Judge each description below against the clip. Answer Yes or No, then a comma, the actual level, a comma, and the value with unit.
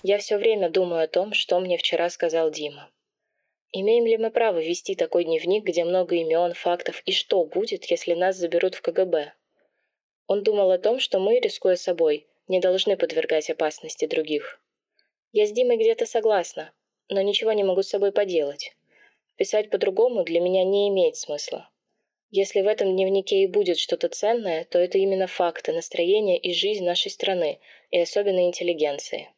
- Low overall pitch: No, high, 200 Hz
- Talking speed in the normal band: No, fast, 170 wpm